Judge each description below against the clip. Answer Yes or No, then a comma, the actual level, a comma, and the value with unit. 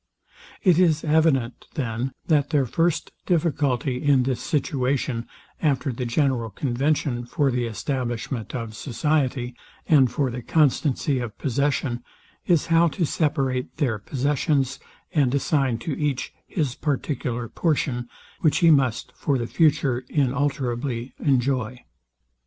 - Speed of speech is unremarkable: No, slow, 125 wpm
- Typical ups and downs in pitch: Yes, average, 3.3 semitones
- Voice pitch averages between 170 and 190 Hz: No, low, 135 Hz